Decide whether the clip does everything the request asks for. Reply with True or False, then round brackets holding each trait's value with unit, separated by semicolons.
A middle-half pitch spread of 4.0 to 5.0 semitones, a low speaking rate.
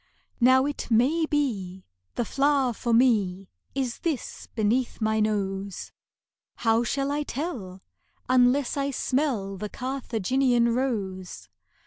True (4.5 semitones; 115 wpm)